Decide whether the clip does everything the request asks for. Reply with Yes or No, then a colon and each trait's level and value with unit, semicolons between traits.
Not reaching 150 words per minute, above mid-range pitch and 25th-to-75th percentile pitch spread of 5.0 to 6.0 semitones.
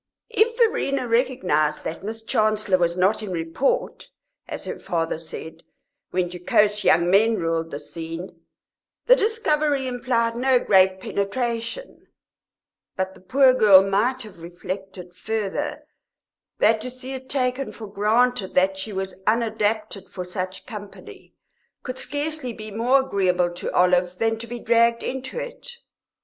Yes: average, 140 wpm; high, 215 Hz; wide, 5.4 semitones